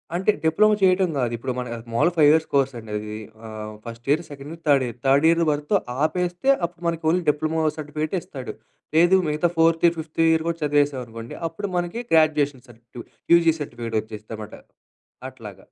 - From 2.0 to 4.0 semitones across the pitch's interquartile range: No, average, 5.1 semitones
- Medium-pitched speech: Yes, medium, 150 Hz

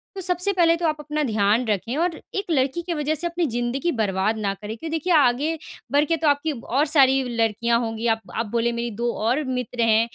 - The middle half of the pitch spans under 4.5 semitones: No, wide, 5.6 semitones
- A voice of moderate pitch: No, very high, 260 Hz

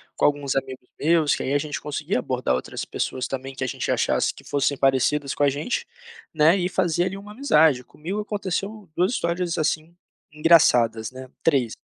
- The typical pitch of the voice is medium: Yes, medium, 150 Hz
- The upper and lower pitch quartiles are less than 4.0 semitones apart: No, average, 4.7 semitones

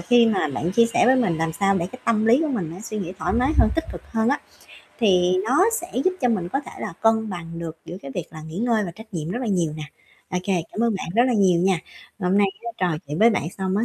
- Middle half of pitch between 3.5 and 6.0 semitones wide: Yes, average, 5.1 semitones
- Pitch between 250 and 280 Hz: No, high, 200 Hz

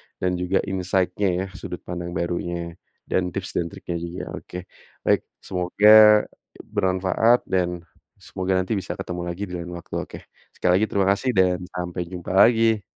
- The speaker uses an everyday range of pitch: No, narrow, 2.0 semitones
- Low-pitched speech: Yes, very low, 90 Hz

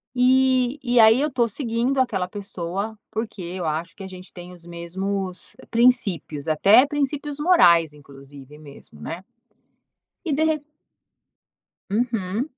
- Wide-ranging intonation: Yes, wide, 6.7 semitones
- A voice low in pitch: No, high, 200 Hz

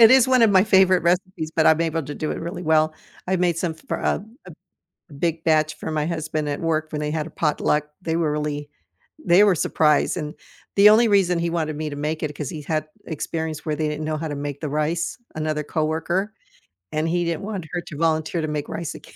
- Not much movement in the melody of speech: Yes, narrow, 2.2 semitones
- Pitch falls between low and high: Yes, medium, 160 Hz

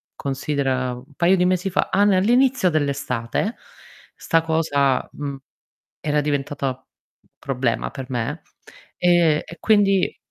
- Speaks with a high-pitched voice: No, medium, 150 Hz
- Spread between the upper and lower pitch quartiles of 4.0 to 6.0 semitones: Yes, average, 5.0 semitones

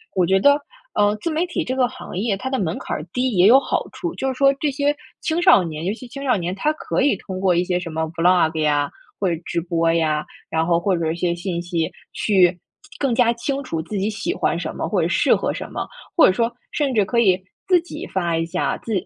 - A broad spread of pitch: Yes, wide, 7.4 semitones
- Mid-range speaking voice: No, high, 195 Hz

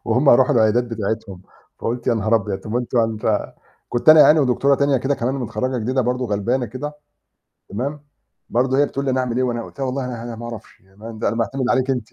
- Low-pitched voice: Yes, low, 120 Hz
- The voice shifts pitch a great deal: No, average, 2.7 semitones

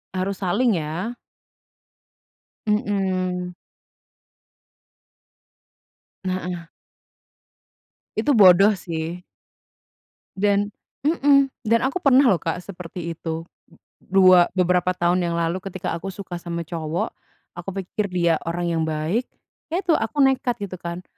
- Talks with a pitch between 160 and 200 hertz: Yes, medium, 185 Hz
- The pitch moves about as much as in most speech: Yes, average, 3.2 semitones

